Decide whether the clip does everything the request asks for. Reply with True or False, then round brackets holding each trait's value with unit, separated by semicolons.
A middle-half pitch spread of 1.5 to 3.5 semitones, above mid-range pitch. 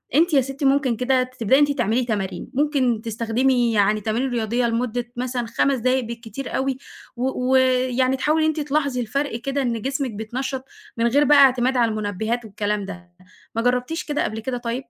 True (2.8 semitones; 250 Hz)